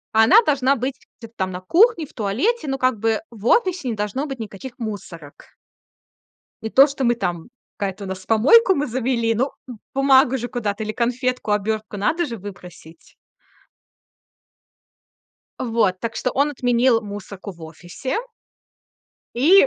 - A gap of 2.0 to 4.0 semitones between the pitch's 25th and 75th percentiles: No, average, 4.7 semitones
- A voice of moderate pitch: No, high, 235 Hz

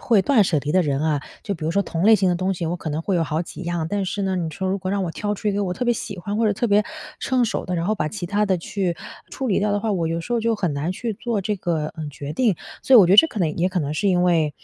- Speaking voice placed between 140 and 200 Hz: Yes, medium, 185 Hz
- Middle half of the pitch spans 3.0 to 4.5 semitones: Yes, average, 3.8 semitones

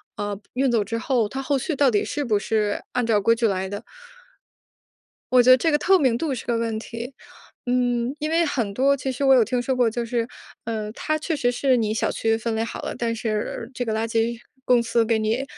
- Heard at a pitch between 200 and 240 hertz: Yes, high, 235 Hz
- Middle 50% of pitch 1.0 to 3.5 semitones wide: Yes, average, 2.9 semitones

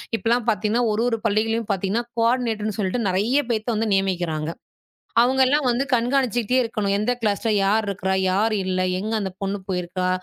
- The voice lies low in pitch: No, high, 215 Hz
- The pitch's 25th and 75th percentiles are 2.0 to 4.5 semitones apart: Yes, average, 3.3 semitones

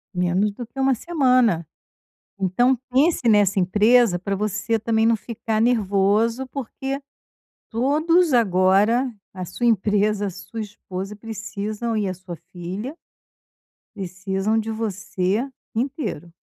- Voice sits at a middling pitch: No, high, 215 Hz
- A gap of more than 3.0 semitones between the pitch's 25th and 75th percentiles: Yes, average, 3.9 semitones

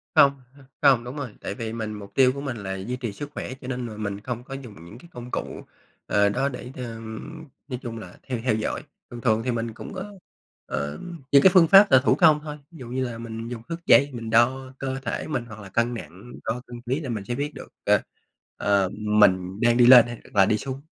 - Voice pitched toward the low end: Yes, low, 120 Hz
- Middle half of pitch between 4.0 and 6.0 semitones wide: No, average, 3.6 semitones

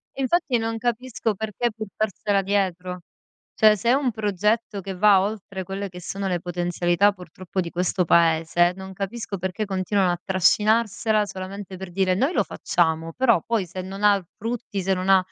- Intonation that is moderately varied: Yes, average, 3.0 semitones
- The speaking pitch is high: Yes, high, 195 Hz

